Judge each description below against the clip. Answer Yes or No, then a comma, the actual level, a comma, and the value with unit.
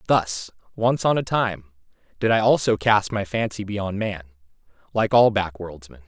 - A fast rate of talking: No, average, 160 wpm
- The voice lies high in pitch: No, low, 100 Hz